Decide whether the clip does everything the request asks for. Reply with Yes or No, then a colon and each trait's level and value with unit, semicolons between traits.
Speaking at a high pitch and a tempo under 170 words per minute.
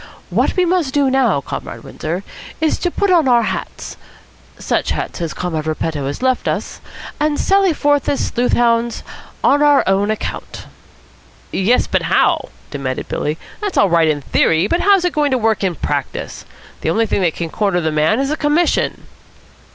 No: high, 230 Hz; average, 180 wpm